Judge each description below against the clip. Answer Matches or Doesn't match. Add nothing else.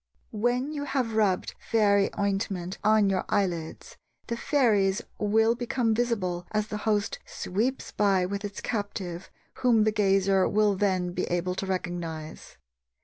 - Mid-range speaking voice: Doesn't match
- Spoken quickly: Doesn't match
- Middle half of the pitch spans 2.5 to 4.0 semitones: Matches